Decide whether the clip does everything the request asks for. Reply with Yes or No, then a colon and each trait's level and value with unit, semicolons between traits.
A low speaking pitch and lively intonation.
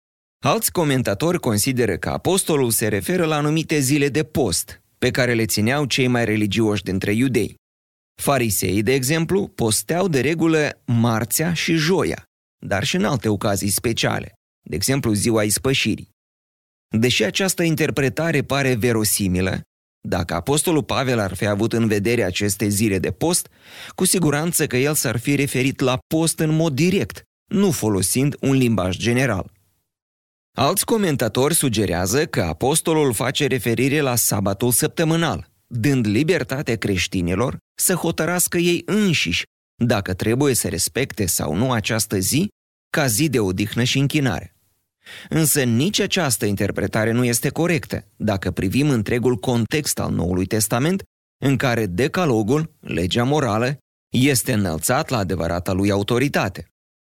Yes: low, 125 Hz; wide, 6.2 semitones